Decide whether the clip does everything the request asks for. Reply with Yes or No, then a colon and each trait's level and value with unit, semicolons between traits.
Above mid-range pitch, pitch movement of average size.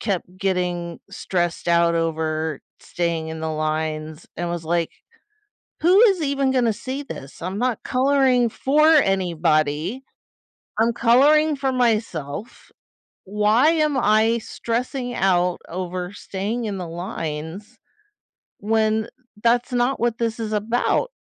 No: high, 210 Hz; wide, 6.3 semitones